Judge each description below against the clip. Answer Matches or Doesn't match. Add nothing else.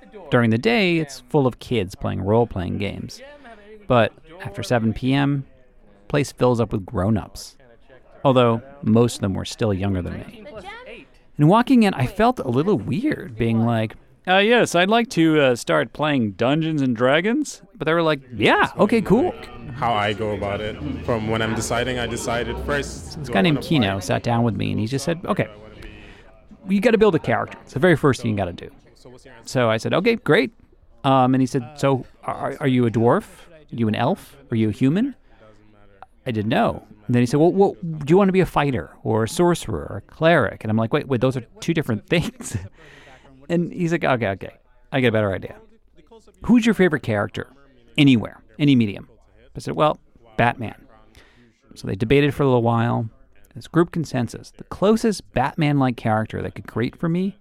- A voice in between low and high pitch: Doesn't match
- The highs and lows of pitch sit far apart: Matches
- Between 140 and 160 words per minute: Doesn't match